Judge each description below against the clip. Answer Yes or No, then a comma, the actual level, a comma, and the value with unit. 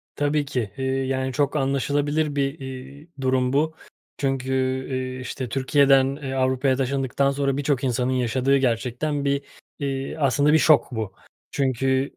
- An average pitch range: No, narrow, 1.4 semitones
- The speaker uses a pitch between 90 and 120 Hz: No, low, 135 Hz